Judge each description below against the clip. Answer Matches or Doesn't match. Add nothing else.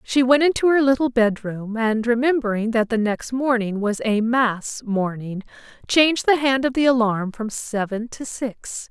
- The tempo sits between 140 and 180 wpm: Matches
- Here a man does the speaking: Doesn't match